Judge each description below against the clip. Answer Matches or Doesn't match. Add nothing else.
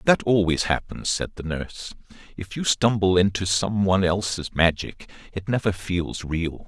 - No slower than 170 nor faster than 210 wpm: Doesn't match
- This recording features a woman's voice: Doesn't match